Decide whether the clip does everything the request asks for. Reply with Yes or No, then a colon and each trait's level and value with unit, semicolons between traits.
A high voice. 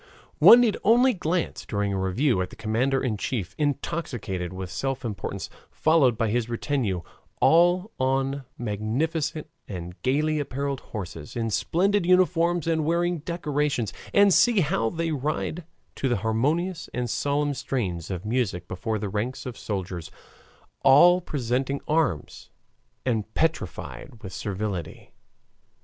No: low, 130 Hz